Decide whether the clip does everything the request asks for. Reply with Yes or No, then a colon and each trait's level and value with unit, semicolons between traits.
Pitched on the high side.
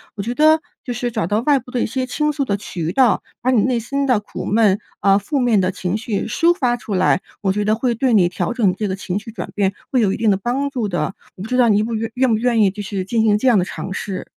Yes: high, 220 Hz